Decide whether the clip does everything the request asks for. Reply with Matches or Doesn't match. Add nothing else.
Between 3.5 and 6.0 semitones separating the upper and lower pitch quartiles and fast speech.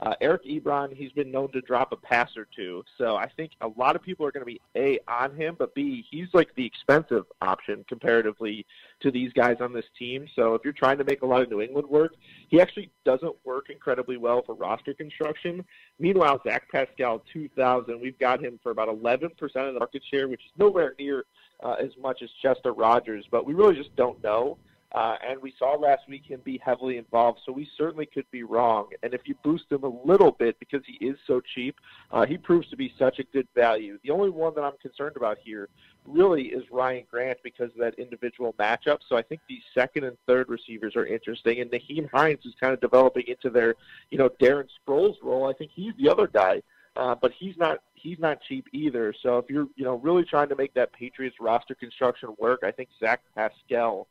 Matches